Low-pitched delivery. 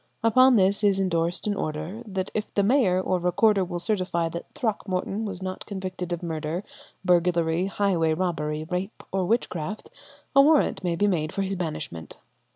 No: medium, 185 Hz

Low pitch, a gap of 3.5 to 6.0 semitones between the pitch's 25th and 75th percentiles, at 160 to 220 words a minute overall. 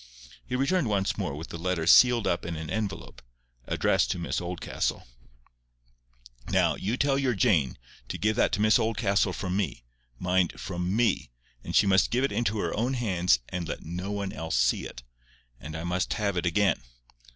Yes: very low, 95 Hz; average, 4.3 semitones; average, 185 wpm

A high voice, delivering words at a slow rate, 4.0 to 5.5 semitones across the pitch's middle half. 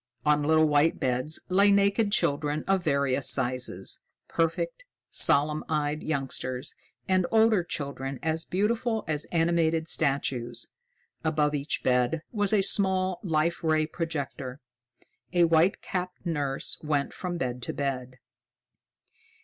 No: medium, 155 Hz; slow, 125 wpm; average, 4.3 semitones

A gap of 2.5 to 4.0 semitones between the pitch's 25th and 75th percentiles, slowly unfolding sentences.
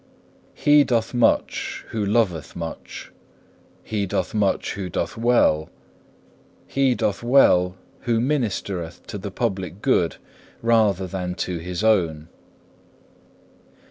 No: average, 4.5 semitones; slow, 115 wpm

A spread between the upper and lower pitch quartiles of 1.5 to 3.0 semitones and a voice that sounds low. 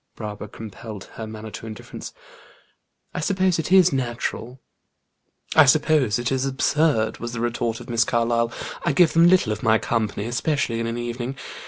No: average, 4.3 semitones; low, 120 Hz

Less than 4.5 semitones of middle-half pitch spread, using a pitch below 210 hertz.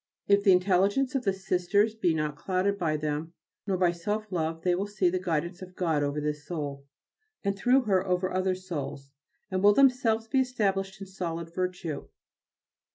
Yes: average, 3.3 semitones; medium, 185 Hz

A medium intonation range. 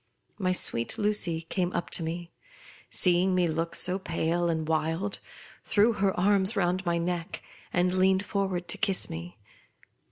No: narrow, 2.3 semitones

